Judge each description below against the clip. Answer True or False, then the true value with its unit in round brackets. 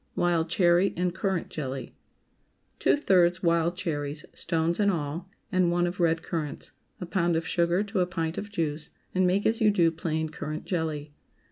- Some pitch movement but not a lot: False (2.2 semitones)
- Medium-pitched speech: True (170 Hz)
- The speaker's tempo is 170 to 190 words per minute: True (180 wpm)